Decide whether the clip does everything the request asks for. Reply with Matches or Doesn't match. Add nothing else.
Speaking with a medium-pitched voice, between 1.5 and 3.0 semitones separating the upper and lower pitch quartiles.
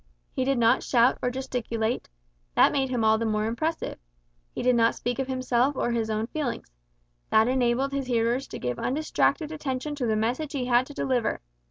Doesn't match